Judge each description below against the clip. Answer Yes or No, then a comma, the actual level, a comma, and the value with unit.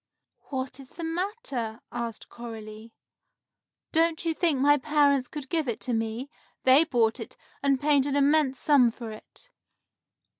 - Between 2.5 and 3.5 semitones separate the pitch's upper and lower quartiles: No, average, 4.3 semitones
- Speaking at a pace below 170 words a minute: Yes, average, 150 wpm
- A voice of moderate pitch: No, very high, 270 Hz